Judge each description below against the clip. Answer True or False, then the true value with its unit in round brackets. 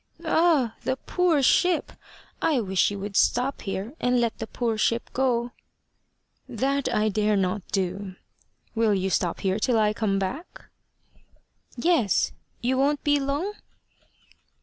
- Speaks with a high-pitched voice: True (235 Hz)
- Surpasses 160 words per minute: False (140 wpm)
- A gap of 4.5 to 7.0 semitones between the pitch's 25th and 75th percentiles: True (5.4 semitones)